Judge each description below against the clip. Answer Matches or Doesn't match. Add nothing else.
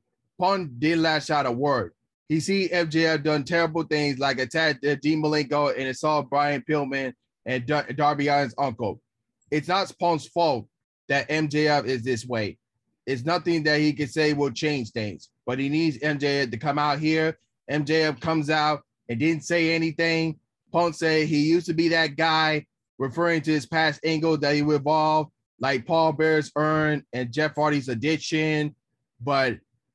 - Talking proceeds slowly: Doesn't match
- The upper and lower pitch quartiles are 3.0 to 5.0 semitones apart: Doesn't match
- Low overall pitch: Doesn't match